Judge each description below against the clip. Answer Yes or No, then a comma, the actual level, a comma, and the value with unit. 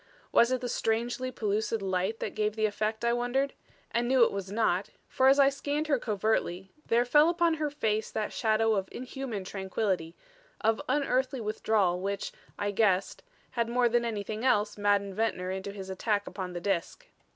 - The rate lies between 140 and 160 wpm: No, average, 180 wpm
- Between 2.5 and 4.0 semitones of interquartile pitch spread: Yes, average, 3.6 semitones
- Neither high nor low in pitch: No, high, 220 Hz